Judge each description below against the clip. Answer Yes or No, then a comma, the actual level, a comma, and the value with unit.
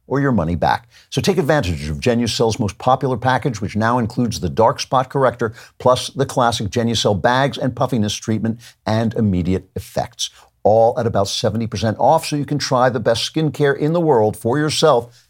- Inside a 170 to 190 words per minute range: Yes, average, 185 wpm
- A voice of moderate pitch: No, low, 120 Hz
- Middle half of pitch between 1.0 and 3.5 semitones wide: Yes, average, 3.1 semitones